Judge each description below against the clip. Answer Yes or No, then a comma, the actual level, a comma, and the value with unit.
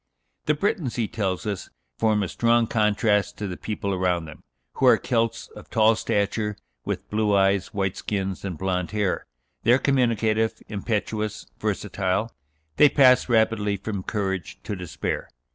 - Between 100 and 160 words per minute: Yes, average, 155 wpm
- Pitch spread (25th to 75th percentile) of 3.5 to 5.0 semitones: No, average, 2.7 semitones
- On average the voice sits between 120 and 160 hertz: No, low, 105 Hz